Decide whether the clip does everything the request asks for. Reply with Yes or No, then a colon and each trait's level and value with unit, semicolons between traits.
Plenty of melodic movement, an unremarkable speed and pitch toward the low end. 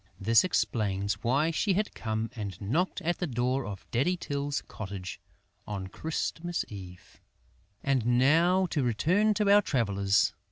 Yes: wide, 8.6 semitones; average, 145 wpm; low, 125 Hz